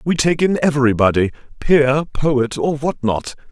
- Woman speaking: No, male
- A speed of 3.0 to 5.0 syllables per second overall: Yes, 4.5 syllables/s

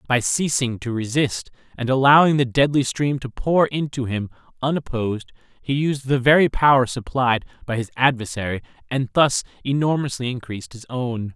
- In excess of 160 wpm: No, average, 155 wpm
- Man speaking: Yes, male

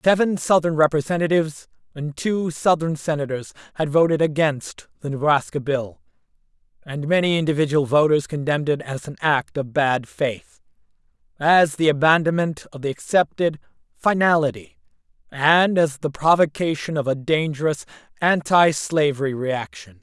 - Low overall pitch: No, medium, 150 Hz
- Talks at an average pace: No, slow, 120 wpm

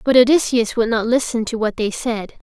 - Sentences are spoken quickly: Yes, fast, 210 wpm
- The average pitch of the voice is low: No, high, 230 Hz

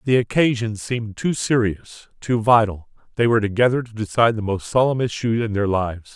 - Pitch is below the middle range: Yes, low, 110 Hz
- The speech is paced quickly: No, average, 185 wpm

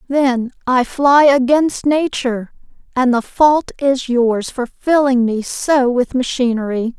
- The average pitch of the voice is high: Yes, very high, 260 Hz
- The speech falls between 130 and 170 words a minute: Yes, slow, 135 wpm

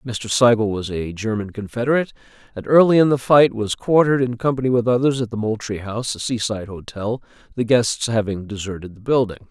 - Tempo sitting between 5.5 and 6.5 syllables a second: Yes, 5.9 syllables/s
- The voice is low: Yes, low, 115 Hz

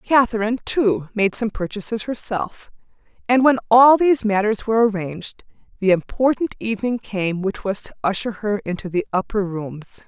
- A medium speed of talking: Yes, average, 155 wpm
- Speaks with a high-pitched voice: Yes, high, 215 Hz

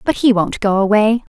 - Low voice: No, high, 215 Hz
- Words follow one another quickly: Yes, fast, 225 wpm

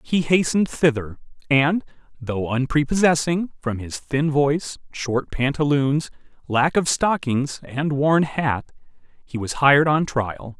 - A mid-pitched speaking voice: Yes, medium, 145 Hz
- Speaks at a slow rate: Yes, slow, 130 wpm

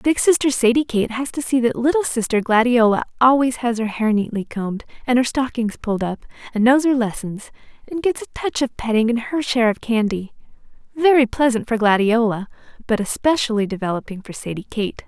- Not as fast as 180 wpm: No, average, 185 wpm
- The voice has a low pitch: No, high, 240 Hz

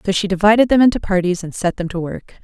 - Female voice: Yes, female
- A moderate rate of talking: No, fast, 270 wpm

